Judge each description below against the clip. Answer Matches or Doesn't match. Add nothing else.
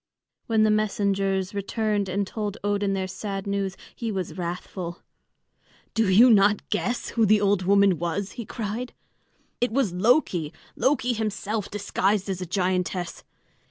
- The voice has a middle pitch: Doesn't match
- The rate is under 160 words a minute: Matches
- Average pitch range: Doesn't match